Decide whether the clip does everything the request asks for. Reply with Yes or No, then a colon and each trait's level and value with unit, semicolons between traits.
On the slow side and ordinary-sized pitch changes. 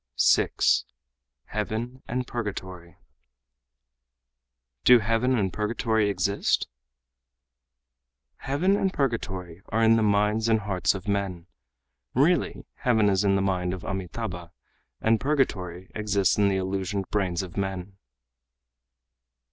Yes: slow, 115 wpm; average, 3.3 semitones